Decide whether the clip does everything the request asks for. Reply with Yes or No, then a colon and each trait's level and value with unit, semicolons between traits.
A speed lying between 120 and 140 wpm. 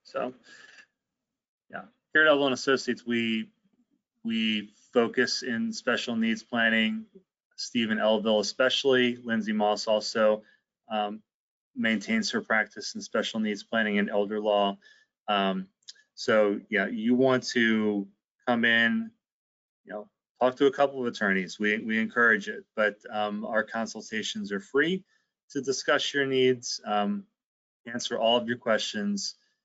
Yes: slow, 135 wpm